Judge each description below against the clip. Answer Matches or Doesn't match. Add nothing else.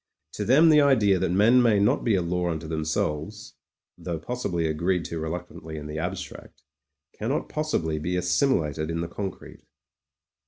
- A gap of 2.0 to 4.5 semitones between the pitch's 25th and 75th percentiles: Doesn't match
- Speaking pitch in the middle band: Doesn't match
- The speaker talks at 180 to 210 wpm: Matches